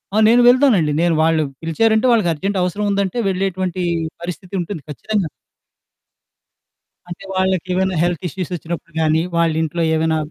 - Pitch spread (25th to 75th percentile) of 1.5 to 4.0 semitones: Yes, average, 3.2 semitones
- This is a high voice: No, medium, 180 Hz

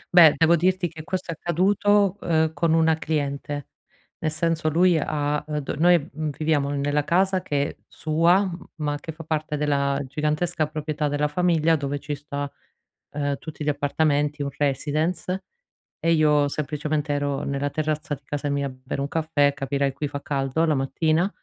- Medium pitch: Yes, medium, 150 Hz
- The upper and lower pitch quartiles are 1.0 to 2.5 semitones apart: Yes, narrow, 2.2 semitones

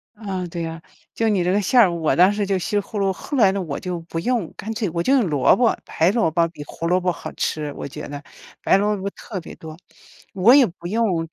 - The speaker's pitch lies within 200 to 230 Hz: No, medium, 185 Hz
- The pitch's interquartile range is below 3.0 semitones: No, average, 3.9 semitones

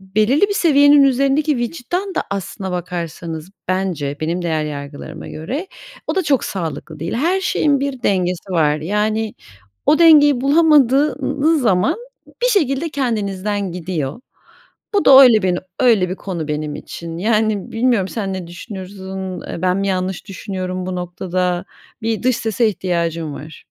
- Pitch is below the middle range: No, high, 195 Hz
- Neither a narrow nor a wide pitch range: No, wide, 7.0 semitones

